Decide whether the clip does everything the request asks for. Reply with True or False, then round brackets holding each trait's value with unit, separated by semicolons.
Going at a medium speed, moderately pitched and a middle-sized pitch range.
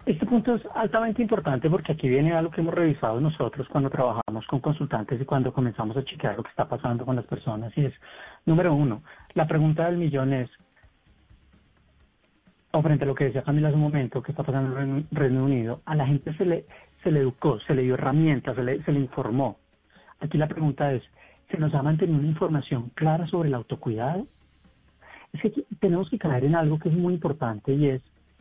False (210 wpm; 145 Hz; 3.7 semitones)